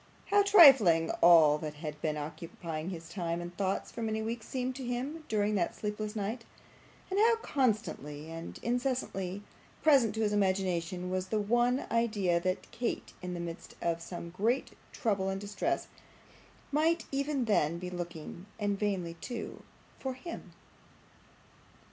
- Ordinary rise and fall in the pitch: No, wide, 6.0 semitones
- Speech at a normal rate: Yes, average, 150 wpm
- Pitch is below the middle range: No, high, 205 Hz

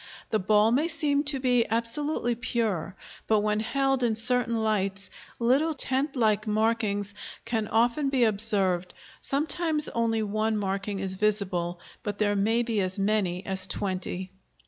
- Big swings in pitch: No, average, 3.5 semitones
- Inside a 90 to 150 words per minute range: Yes, average, 145 wpm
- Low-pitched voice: No, high, 220 Hz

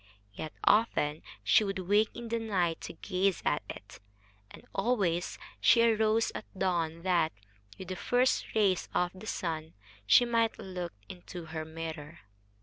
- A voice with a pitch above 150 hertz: Yes, medium, 185 Hz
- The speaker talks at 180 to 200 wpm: No, average, 150 wpm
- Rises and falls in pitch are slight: No, average, 4.7 semitones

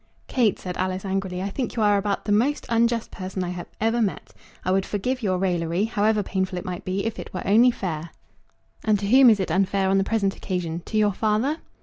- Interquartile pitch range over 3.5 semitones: No, average, 3.0 semitones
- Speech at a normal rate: No, fast, 225 wpm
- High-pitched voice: Yes, high, 200 Hz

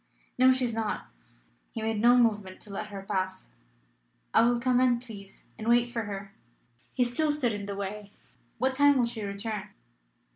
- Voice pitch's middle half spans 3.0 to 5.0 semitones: Yes, average, 3.3 semitones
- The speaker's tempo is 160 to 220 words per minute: Yes, average, 185 wpm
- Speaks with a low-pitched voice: No, high, 225 Hz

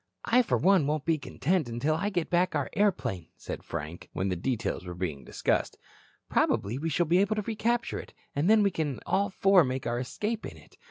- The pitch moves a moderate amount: No, wide, 8.7 semitones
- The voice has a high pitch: No, medium, 160 Hz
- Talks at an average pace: No, fast, 215 wpm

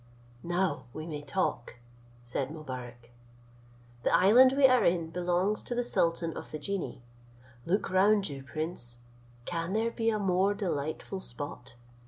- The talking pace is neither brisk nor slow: Yes, average, 145 wpm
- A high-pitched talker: No, medium, 170 Hz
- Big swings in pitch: Yes, wide, 5.7 semitones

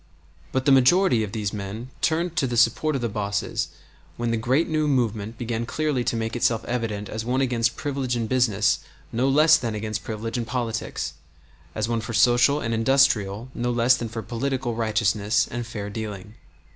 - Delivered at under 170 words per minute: No, average, 185 wpm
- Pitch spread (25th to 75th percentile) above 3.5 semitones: No, average, 2.8 semitones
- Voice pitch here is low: Yes, low, 115 Hz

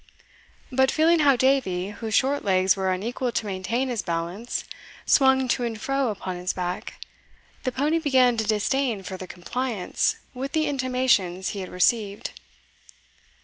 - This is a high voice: Yes, high, 235 Hz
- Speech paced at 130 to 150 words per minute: Yes, average, 145 wpm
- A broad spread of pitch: Yes, wide, 5.7 semitones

